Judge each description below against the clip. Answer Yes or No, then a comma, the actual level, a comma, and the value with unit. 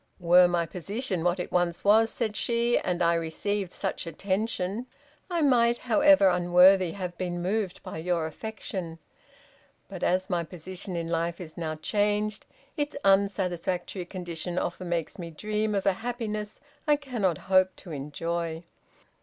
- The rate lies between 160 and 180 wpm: No, average, 150 wpm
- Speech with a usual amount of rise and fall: Yes, average, 3.6 semitones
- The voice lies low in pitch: No, medium, 185 Hz